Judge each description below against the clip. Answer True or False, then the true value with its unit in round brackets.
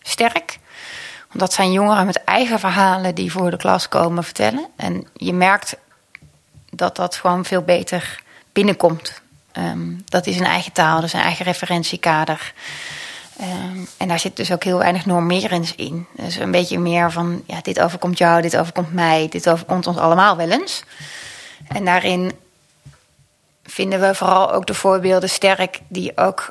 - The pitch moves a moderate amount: False (1.8 semitones)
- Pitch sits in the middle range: True (180 Hz)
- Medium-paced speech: True (165 wpm)